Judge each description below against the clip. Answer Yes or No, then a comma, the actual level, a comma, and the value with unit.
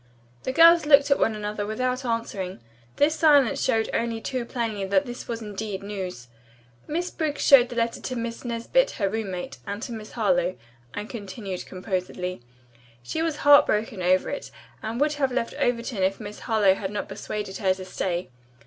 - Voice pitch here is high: Yes, high, 225 Hz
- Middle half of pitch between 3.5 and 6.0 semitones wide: Yes, average, 4.8 semitones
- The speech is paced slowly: No, average, 175 wpm